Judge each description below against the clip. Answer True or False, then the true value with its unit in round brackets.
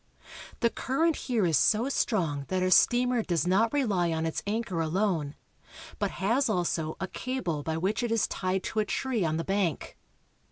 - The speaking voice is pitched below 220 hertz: True (190 Hz)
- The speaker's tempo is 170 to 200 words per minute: True (185 wpm)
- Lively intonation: True (5.9 semitones)